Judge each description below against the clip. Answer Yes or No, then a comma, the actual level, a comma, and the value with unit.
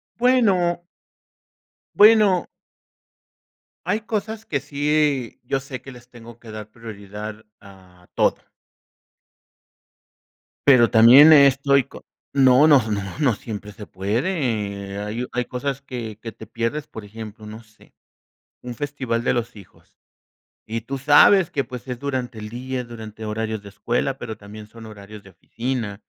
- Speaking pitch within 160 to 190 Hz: No, low, 120 Hz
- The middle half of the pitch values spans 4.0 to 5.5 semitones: Yes, average, 4.4 semitones